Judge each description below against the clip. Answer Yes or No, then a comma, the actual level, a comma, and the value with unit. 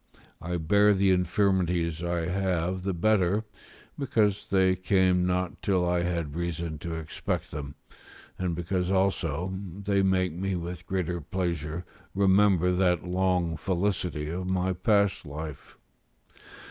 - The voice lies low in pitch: Yes, very low, 90 Hz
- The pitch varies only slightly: Yes, narrow, 1.9 semitones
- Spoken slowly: Yes, slow, 130 wpm